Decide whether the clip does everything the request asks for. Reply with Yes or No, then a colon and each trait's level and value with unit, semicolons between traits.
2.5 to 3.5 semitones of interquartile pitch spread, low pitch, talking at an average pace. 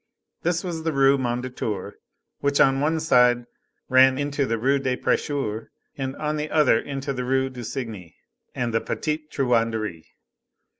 Yes: average, 3.2 semitones; low, 130 Hz; average, 155 wpm